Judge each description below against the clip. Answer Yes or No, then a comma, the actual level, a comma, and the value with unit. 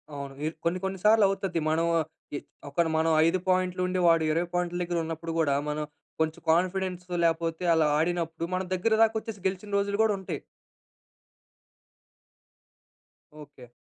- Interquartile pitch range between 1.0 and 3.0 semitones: Yes, narrow, 2.5 semitones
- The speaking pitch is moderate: Yes, medium, 175 Hz